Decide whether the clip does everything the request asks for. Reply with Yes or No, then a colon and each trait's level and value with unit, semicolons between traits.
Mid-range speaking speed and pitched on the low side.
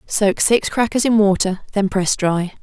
No: average, 185 wpm; high, 200 Hz